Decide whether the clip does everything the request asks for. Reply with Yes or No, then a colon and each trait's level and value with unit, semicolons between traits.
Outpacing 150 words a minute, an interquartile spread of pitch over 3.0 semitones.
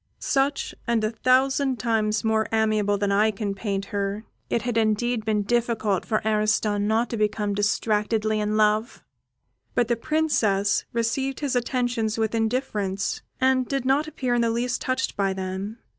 No: average, 165 wpm; narrow, 2.6 semitones